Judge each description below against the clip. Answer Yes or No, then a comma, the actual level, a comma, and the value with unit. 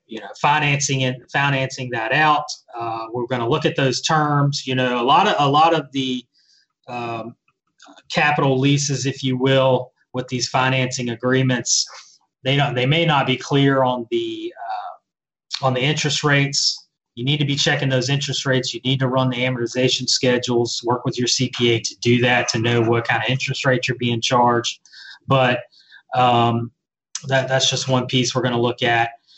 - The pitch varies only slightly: Yes, narrow, 2.3 semitones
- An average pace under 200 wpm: Yes, average, 190 wpm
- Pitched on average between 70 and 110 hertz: No, low, 130 Hz